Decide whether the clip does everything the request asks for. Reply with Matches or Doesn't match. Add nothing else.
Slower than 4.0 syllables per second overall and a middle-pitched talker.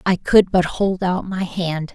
Matches